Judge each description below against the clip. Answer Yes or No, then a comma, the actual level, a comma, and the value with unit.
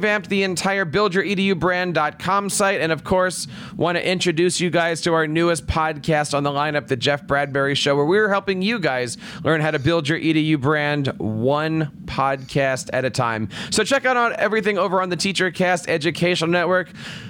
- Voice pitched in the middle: Yes, medium, 170 Hz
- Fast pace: No, average, 185 wpm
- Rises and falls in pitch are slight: No, average, 4.4 semitones